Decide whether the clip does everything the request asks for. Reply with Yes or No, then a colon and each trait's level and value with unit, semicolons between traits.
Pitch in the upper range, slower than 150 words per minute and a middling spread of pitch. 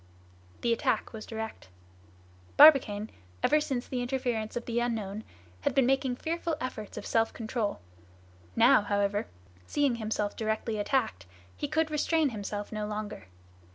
Yes: high, 230 Hz; average, 140 wpm; average, 3.9 semitones